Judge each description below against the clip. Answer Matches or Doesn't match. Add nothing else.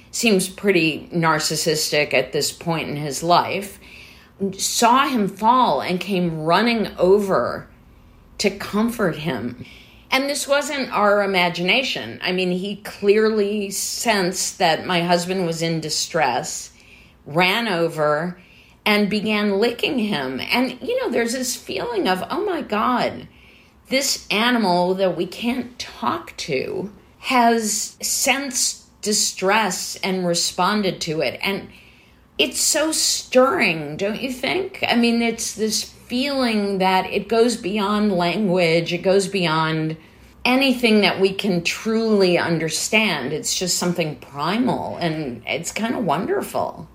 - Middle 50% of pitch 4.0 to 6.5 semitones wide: Matches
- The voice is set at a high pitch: Matches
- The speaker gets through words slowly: Matches